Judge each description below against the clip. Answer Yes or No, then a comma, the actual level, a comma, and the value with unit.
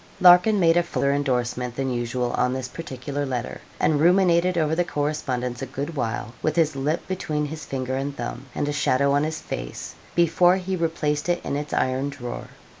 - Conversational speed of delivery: Yes, average, 190 wpm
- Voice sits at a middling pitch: Yes, medium, 145 Hz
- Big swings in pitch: No, average, 4.4 semitones